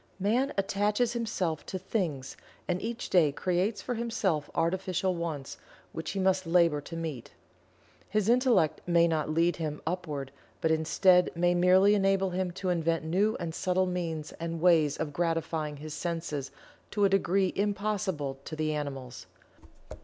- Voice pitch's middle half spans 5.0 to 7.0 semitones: No, average, 3.5 semitones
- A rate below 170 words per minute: Yes, average, 155 wpm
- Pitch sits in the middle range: Yes, medium, 175 Hz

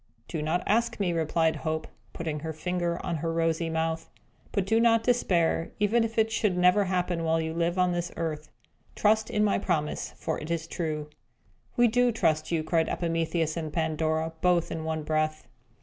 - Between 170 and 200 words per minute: Yes, average, 185 wpm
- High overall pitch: No, medium, 165 Hz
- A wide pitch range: No, narrow, 2.6 semitones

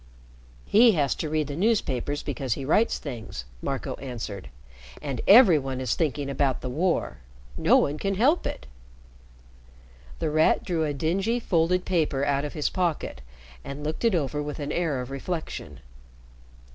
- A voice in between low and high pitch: Yes, medium, 150 Hz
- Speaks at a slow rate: No, average, 160 wpm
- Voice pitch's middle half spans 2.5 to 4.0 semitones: No, average, 4.4 semitones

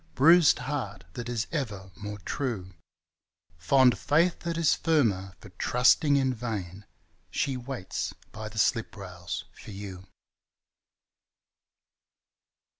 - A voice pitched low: Yes, low, 115 Hz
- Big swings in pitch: Yes, wide, 5.9 semitones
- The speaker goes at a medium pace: No, slow, 115 wpm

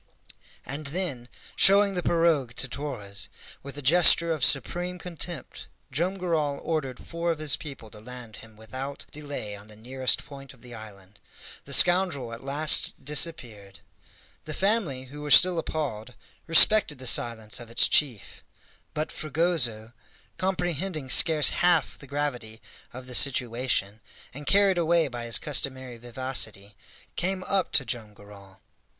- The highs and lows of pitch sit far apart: Yes, wide, 5.9 semitones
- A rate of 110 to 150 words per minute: Yes, average, 145 wpm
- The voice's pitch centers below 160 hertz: Yes, medium, 140 Hz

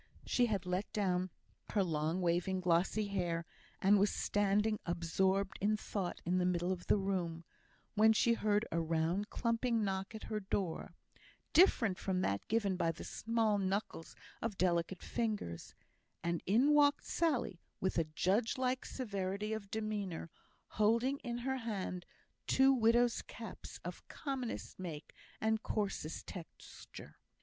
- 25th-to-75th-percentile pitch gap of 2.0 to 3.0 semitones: No, average, 3.6 semitones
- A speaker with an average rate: Yes, average, 145 wpm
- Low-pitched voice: No, high, 200 Hz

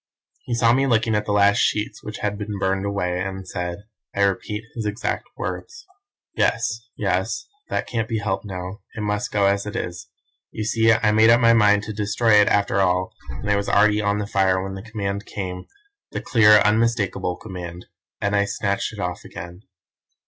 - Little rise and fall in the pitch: Yes, narrow, 2.2 semitones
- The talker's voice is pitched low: Yes, low, 105 Hz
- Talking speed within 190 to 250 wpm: Yes, average, 195 wpm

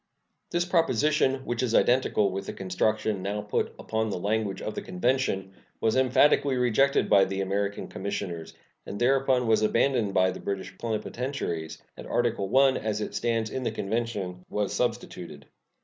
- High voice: No, low, 110 Hz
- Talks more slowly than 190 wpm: Yes, average, 160 wpm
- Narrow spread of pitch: No, average, 4.4 semitones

